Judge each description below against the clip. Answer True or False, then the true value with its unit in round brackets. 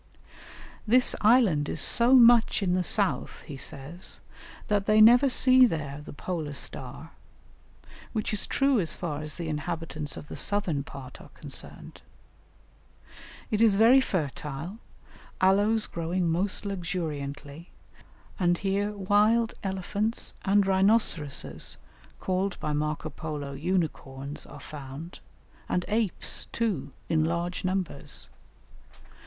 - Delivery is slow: True (120 wpm)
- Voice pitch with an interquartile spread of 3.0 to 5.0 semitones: False (5.5 semitones)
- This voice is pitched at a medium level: True (180 Hz)